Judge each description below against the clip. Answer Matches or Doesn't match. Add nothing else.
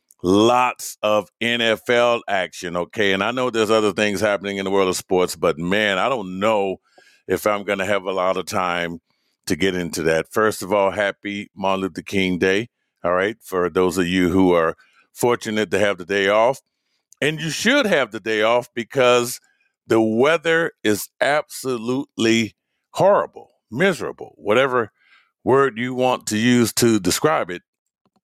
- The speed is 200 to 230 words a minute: Doesn't match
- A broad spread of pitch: Doesn't match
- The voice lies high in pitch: Doesn't match